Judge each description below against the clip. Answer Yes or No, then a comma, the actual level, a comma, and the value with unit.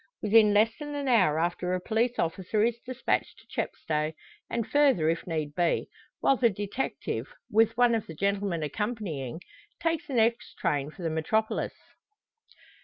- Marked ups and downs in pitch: Yes, wide, 6.1 semitones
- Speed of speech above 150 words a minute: Yes, average, 160 wpm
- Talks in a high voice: Yes, high, 210 Hz